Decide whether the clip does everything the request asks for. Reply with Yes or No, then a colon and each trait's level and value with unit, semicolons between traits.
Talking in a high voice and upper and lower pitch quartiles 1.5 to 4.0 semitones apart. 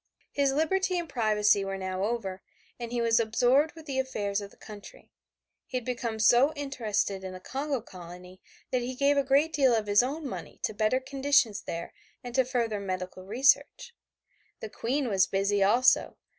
No: high, 235 Hz; average, 5.1 semitones